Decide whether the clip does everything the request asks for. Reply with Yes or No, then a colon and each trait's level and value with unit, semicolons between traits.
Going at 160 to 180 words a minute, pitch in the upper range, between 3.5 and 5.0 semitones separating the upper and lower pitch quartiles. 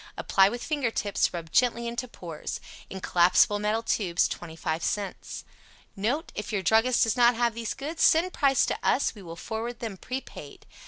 Yes: average, 175 wpm; high, 225 Hz; average, 4.2 semitones